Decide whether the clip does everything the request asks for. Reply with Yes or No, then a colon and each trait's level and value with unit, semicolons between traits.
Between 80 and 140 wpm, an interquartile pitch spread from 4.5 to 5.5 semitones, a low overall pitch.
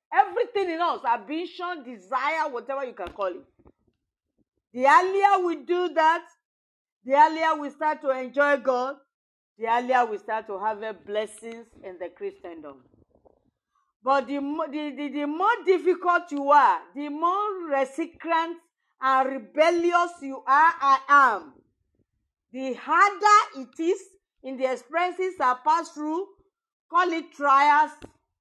No: slow, 135 wpm; average, 5.0 semitones; very high, 300 Hz